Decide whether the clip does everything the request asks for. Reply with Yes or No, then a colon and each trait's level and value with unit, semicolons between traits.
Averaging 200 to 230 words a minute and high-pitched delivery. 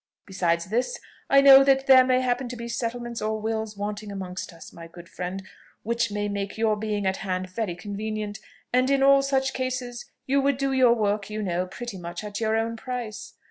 Yes: fast, 205 wpm; high, 220 Hz